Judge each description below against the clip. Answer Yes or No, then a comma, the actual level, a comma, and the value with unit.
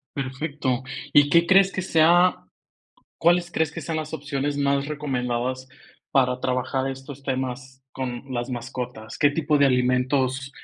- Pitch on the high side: No, low, 135 Hz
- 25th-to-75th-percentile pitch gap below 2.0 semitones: No, average, 2.9 semitones